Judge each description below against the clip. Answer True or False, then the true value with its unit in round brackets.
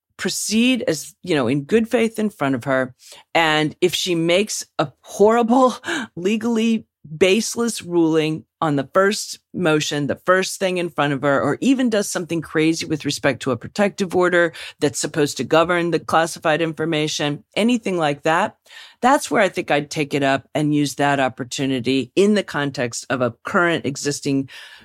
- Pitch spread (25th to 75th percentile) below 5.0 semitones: False (5.4 semitones)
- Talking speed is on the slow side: False (170 wpm)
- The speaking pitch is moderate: True (160 Hz)